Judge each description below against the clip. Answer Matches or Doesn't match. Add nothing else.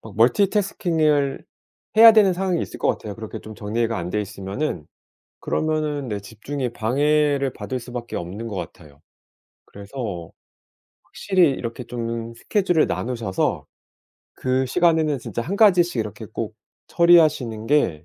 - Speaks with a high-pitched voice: Doesn't match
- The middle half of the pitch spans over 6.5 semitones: Doesn't match